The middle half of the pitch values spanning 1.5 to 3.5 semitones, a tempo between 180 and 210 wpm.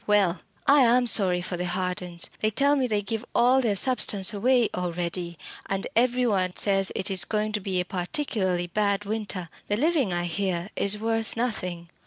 No: average, 3.9 semitones; average, 185 wpm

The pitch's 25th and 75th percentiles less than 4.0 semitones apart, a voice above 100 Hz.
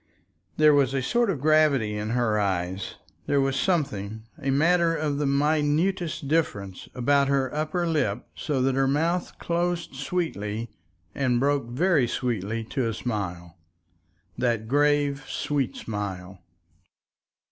No: wide, 5.6 semitones; low, 135 Hz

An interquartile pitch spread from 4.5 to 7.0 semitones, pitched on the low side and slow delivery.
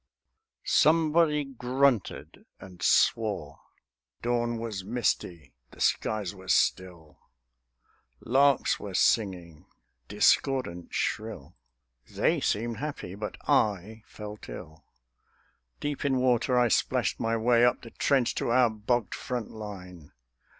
Yes: average, 5.0 semitones; low, 110 Hz; slow, 110 wpm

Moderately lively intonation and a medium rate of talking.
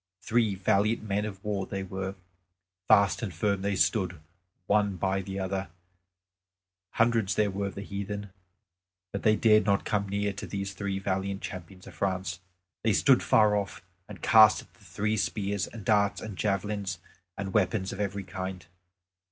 No: narrow, 1.6 semitones; average, 170 wpm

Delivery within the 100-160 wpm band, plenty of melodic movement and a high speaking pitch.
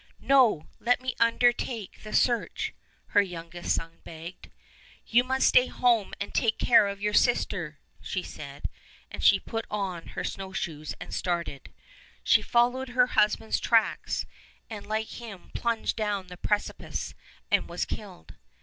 No: average, 150 wpm; average, 5.0 semitones; high, 210 Hz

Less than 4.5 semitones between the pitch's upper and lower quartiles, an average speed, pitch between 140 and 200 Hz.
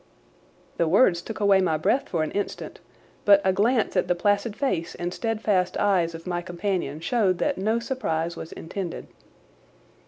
Yes: average, 3.8 semitones; average, 165 wpm; high, 190 Hz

